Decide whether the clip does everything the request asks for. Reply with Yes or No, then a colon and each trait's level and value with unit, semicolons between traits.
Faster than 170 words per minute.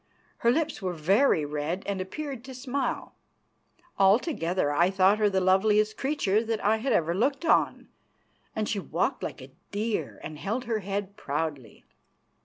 No: average, 160 wpm